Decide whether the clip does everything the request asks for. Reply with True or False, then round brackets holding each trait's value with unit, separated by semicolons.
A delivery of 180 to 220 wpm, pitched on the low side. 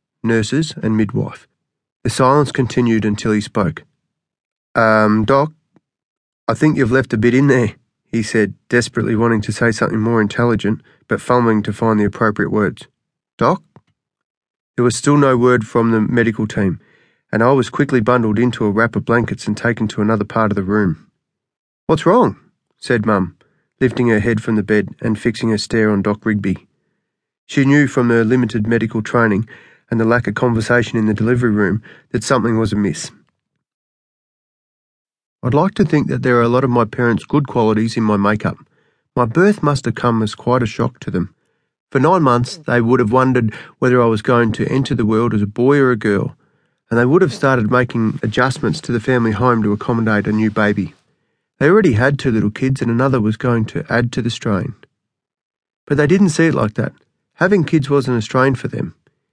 True (195 wpm; 115 Hz)